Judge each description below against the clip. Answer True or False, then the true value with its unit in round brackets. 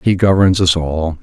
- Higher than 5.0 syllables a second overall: False (4.5 syllables/s)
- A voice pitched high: False (90 Hz)